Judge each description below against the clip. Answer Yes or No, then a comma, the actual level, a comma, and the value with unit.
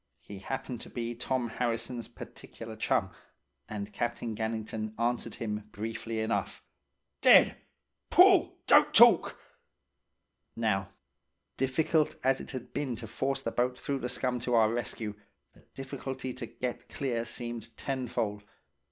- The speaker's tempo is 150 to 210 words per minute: No, slow, 135 wpm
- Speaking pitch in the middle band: No, low, 120 Hz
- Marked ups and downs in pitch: No, narrow, 2.5 semitones